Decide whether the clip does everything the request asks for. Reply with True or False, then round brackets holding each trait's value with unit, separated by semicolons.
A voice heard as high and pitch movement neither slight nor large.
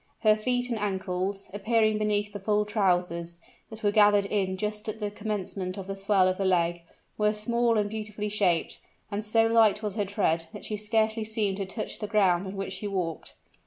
False (205 Hz; 2.0 semitones)